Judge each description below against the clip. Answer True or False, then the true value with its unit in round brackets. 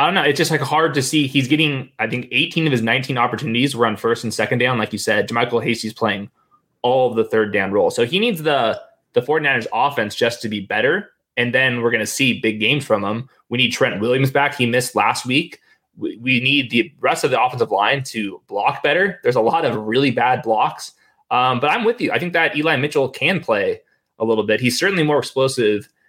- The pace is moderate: False (235 wpm)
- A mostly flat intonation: False (4.5 semitones)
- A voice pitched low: True (125 Hz)